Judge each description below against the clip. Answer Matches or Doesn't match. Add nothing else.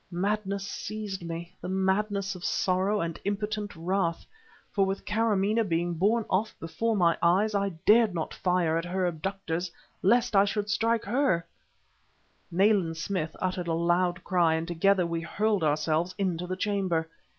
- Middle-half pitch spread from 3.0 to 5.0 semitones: Matches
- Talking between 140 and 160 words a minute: Matches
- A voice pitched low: Doesn't match